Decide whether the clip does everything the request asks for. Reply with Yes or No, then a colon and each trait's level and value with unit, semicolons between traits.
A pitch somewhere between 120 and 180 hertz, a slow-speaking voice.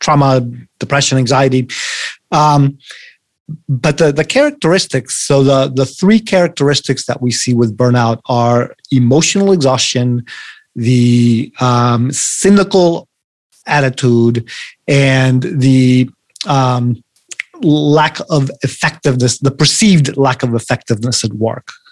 Yes: low, 135 Hz; slow, 105 wpm